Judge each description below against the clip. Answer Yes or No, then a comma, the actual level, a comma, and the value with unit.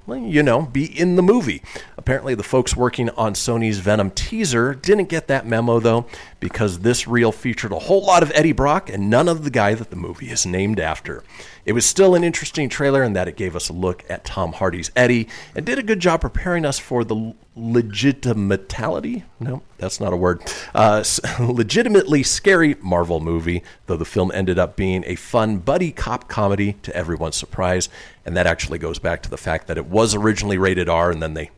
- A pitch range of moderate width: No, wide, 6.8 semitones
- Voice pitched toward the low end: Yes, low, 110 Hz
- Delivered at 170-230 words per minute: Yes, fast, 205 wpm